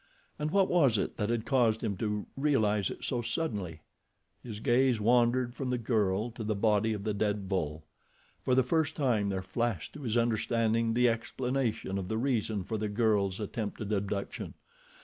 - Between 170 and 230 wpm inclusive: Yes, average, 180 wpm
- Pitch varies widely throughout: No, average, 3.1 semitones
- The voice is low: Yes, low, 110 Hz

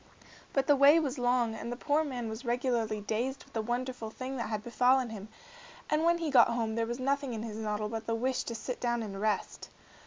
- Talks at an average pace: No, fast, 230 wpm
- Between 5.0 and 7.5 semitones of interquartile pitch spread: No, average, 3.0 semitones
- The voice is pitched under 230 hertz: No, high, 240 Hz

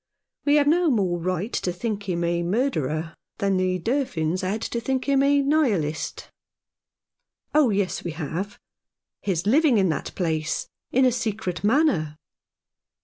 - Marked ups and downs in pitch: Yes, wide, 7.2 semitones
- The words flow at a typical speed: Yes, average, 155 wpm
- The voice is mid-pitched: No, high, 200 Hz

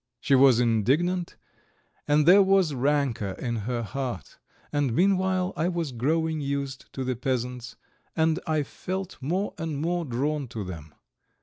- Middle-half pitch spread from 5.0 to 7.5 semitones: Yes, average, 5.3 semitones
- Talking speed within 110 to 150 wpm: Yes, average, 145 wpm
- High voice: No, medium, 140 Hz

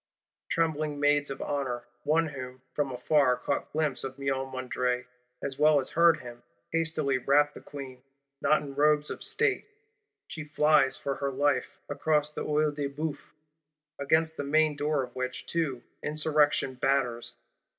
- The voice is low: No, medium, 145 Hz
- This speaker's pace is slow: No, average, 155 wpm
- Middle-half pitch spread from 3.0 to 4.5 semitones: No, narrow, 2.4 semitones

